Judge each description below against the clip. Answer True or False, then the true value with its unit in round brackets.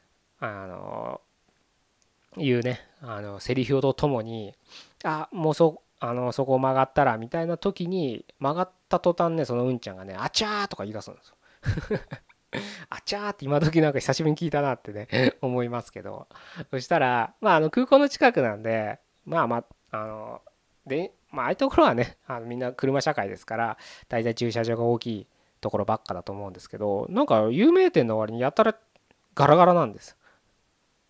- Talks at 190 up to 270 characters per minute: False (355 characters per minute)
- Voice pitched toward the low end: True (130 Hz)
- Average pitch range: False (6.7 semitones)